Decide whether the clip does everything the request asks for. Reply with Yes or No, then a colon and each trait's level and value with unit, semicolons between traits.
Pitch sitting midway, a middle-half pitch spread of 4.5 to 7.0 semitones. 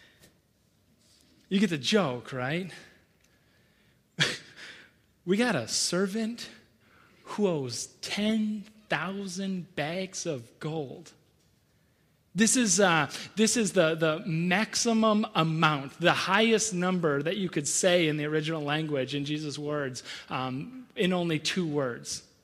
Yes: medium, 170 Hz; average, 5.0 semitones